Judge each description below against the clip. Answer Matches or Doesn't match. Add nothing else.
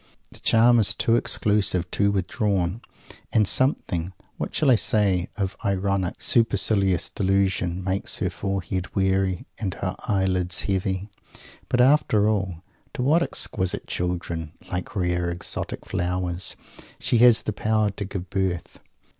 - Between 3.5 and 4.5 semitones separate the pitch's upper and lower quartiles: Doesn't match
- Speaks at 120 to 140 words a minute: Matches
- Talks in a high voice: Doesn't match